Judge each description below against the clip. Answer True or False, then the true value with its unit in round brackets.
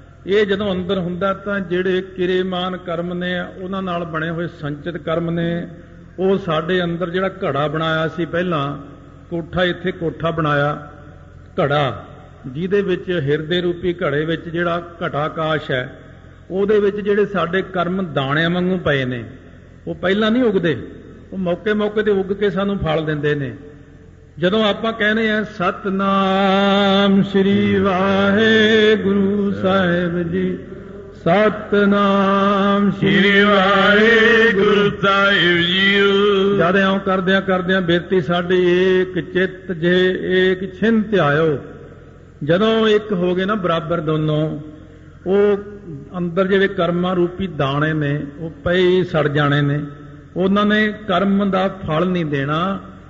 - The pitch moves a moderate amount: True (3.1 semitones)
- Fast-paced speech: False (130 wpm)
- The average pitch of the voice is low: False (185 Hz)